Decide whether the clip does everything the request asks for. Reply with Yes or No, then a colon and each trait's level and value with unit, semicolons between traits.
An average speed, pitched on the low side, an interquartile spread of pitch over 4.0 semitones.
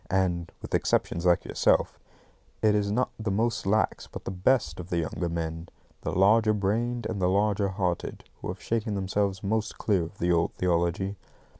No: average, 180 wpm; very low, 95 Hz; average, 3.5 semitones